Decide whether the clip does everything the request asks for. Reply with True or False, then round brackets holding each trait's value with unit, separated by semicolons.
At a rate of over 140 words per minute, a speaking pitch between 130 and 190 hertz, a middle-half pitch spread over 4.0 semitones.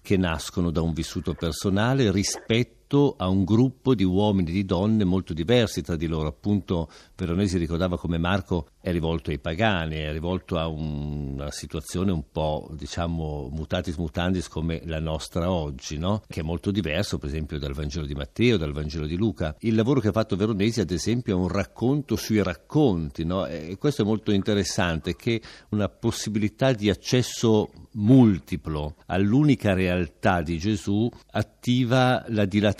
False (165 wpm; 90 Hz; 4.6 semitones)